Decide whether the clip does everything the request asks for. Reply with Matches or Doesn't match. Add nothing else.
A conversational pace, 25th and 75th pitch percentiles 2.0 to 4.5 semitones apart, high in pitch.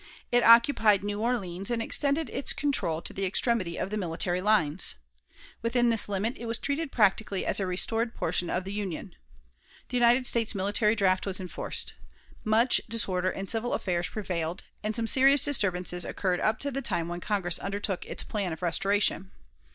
Matches